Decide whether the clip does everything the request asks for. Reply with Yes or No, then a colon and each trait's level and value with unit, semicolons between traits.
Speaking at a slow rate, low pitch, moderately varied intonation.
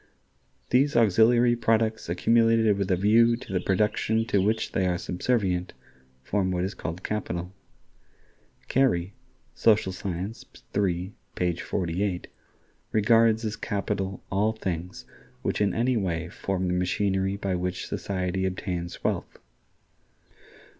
Yes: slow, 125 wpm; low, 100 Hz; average, 3.4 semitones